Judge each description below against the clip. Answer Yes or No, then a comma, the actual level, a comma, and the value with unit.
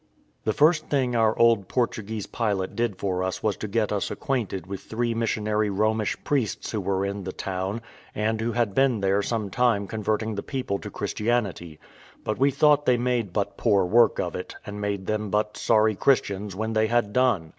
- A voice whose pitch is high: No, low, 110 Hz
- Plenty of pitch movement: No, average, 2.9 semitones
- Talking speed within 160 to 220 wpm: Yes, average, 195 wpm